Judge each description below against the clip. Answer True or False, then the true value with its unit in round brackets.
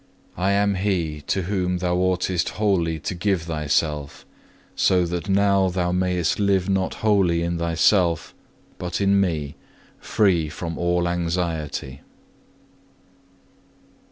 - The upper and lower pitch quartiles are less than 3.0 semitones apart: True (2.4 semitones)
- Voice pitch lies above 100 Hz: False (90 Hz)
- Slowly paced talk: True (120 wpm)